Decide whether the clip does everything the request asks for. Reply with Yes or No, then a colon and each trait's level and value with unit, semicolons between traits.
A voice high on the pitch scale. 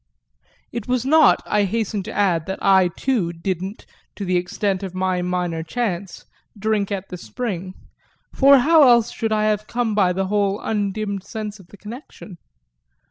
Yes: high, 200 Hz